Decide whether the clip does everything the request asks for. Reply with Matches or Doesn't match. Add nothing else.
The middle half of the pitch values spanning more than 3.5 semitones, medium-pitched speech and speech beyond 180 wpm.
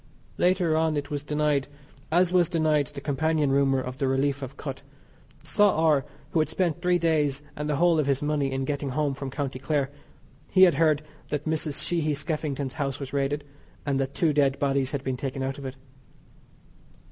Doesn't match